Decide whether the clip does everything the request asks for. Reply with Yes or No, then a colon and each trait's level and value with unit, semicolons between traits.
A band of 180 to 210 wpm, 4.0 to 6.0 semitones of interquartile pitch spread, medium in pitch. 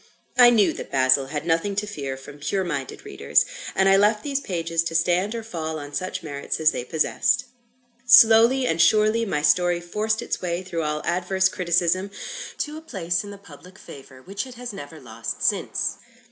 Yes: average, 190 wpm; average, 5.3 semitones; medium, 180 Hz